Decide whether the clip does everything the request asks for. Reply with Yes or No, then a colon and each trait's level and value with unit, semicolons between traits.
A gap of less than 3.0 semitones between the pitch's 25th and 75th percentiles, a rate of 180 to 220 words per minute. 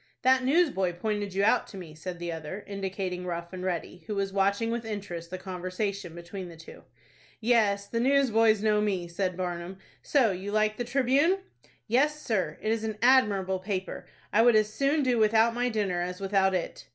No: average, 3.8 semitones; average, 190 wpm